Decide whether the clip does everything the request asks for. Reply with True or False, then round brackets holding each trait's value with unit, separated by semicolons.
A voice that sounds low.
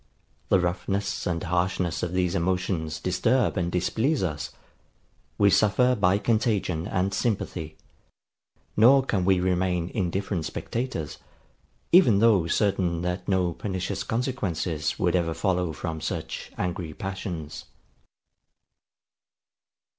True (90 Hz)